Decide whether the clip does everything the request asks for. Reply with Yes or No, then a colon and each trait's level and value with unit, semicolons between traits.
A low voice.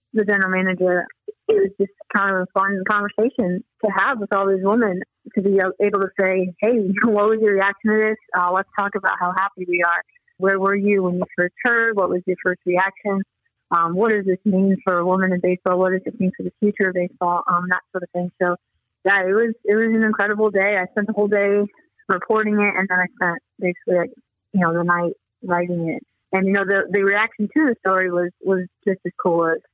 No: high, 195 Hz